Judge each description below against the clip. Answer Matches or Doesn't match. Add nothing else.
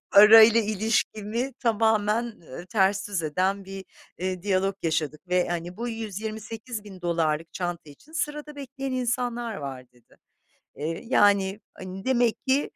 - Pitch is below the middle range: Doesn't match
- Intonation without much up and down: Doesn't match